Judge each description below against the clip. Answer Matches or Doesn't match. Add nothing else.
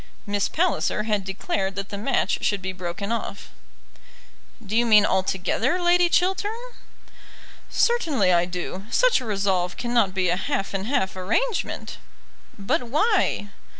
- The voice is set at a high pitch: Matches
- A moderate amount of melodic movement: Doesn't match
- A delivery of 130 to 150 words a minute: Matches